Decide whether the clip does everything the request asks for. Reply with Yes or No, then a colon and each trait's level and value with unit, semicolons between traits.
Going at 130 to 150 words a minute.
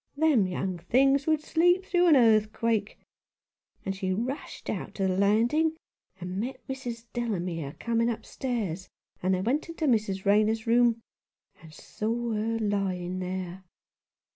Yes: average, 140 wpm